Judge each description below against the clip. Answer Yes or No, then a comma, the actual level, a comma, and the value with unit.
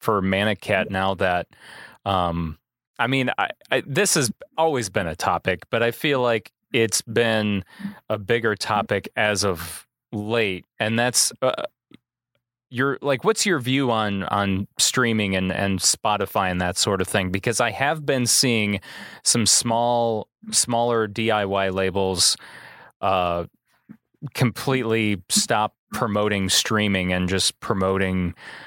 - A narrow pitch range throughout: No, average, 4.0 semitones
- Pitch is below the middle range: Yes, low, 110 Hz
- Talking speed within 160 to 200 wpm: No, slow, 135 wpm